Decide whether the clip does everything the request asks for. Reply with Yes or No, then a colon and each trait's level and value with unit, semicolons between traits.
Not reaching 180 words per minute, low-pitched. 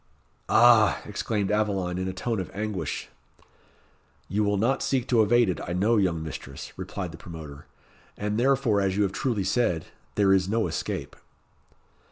Yes: average, 165 wpm; low, 100 Hz